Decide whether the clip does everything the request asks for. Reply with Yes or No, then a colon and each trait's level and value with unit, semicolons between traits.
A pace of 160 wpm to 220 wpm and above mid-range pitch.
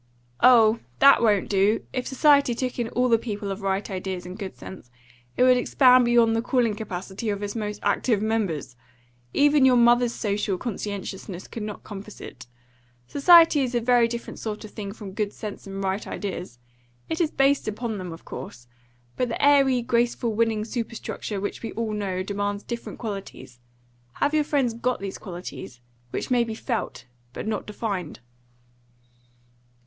Yes: average, 170 wpm; high, 220 Hz